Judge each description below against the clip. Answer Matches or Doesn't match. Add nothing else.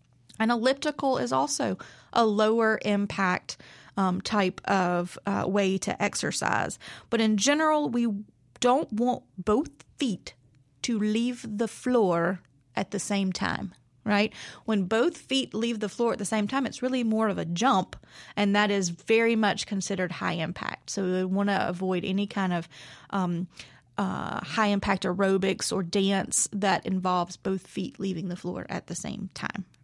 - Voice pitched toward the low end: Doesn't match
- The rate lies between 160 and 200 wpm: Matches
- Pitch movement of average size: Matches